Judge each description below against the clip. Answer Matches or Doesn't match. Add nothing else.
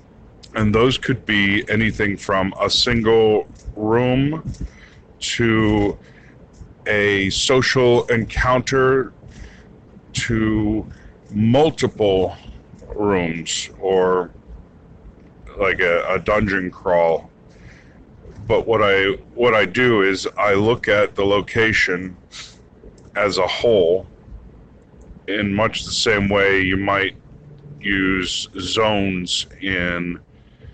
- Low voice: Matches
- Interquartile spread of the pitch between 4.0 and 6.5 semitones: Doesn't match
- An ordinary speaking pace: Doesn't match